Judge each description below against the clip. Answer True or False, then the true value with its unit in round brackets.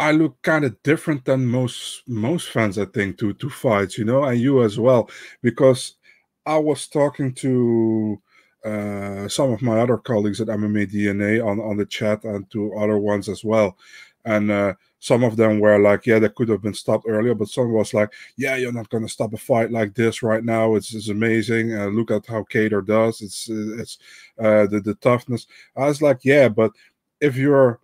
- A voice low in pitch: True (110 Hz)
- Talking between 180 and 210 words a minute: True (205 wpm)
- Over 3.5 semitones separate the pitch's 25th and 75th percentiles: False (3.1 semitones)